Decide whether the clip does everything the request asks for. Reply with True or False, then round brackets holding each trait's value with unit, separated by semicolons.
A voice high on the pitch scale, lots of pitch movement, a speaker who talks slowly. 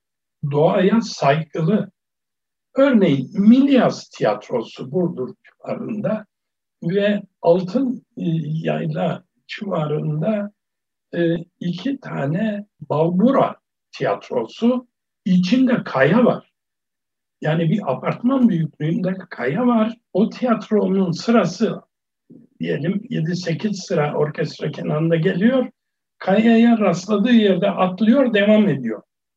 False (195 Hz; 5.0 semitones; 80 wpm)